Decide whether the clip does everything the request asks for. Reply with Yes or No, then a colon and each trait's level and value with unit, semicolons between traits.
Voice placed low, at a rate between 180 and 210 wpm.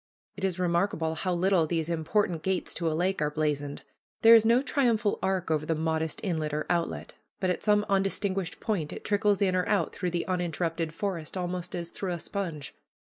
No: medium, 180 Hz; average, 200 wpm